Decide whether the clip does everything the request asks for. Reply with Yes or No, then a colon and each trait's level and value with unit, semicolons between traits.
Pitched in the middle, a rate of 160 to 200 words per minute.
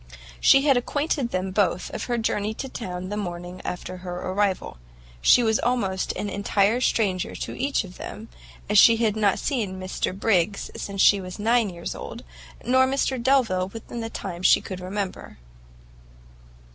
No: high, 205 Hz; average, 170 wpm